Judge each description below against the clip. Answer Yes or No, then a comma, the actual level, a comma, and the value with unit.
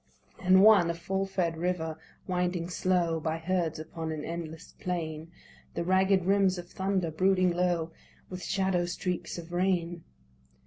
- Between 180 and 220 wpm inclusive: No, average, 145 wpm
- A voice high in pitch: No, medium, 175 Hz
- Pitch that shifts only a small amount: Yes, narrow, 2.1 semitones